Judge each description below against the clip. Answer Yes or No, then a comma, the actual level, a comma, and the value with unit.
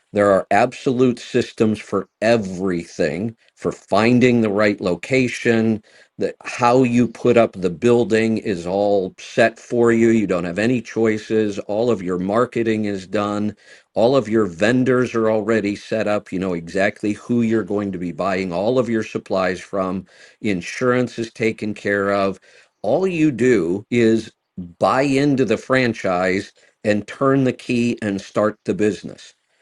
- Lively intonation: No, average, 3.2 semitones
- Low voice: Yes, low, 110 Hz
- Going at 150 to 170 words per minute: Yes, average, 155 wpm